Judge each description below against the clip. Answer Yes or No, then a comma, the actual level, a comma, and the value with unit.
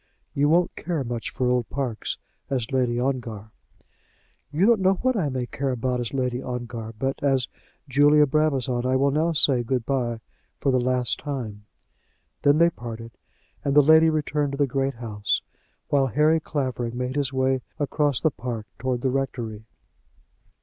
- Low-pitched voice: Yes, low, 130 Hz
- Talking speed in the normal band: Yes, average, 170 wpm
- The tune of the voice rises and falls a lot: No, average, 3.1 semitones